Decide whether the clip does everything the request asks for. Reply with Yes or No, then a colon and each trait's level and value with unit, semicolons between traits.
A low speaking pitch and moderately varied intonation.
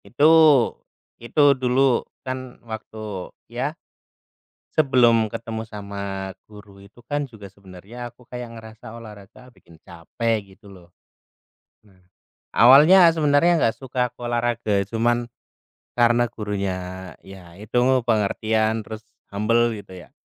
Yes: low, 115 Hz; average, 3.5 semitones